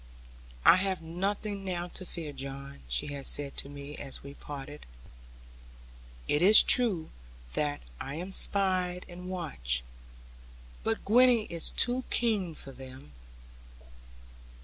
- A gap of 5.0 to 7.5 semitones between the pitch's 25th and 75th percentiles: Yes, wide, 5.6 semitones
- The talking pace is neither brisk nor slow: No, slow, 125 wpm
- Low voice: No, medium, 170 Hz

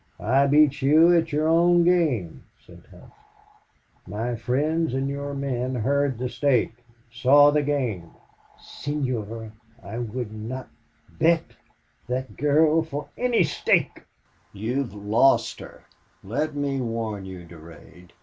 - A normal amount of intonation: Yes, average, 4.7 semitones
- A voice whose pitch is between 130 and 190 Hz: Yes, low, 135 Hz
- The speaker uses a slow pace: Yes, slow, 130 wpm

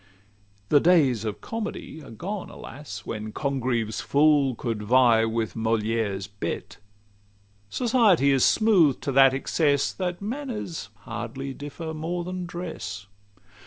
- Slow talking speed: Yes, slow, 125 wpm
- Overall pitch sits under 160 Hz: Yes, low, 135 Hz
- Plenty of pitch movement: Yes, wide, 7.4 semitones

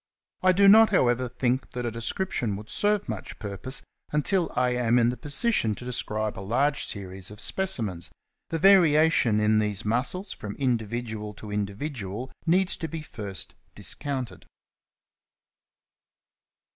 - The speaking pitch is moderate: No, low, 120 Hz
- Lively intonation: Yes, wide, 6.5 semitones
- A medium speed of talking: Yes, average, 145 wpm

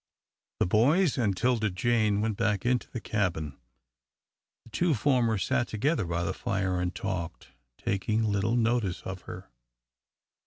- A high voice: No, low, 105 Hz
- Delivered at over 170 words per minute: No, average, 145 wpm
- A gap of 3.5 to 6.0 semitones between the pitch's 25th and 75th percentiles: Yes, average, 4.0 semitones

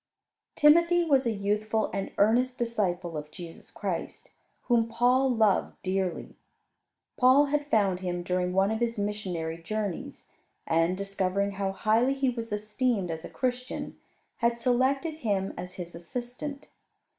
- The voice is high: Yes, high, 215 Hz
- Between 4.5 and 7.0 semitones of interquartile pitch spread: Yes, average, 5.1 semitones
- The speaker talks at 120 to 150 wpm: Yes, average, 140 wpm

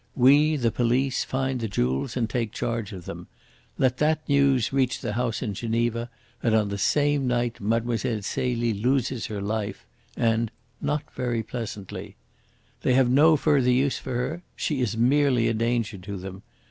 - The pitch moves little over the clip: No, average, 3.0 semitones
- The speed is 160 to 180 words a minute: Yes, average, 170 wpm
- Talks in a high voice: No, low, 120 Hz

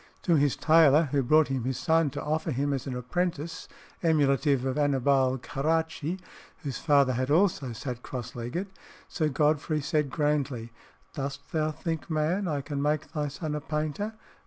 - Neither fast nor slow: Yes, average, 165 wpm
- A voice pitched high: No, medium, 150 Hz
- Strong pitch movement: No, average, 2.8 semitones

